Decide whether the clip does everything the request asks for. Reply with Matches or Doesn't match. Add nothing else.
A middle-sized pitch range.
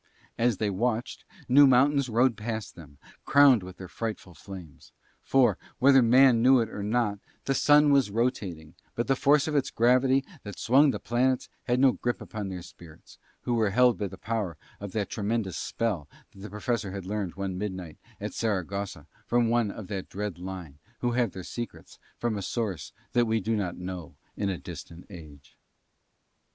Matches